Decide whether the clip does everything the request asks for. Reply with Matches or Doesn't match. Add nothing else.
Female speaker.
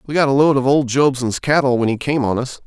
Doesn't match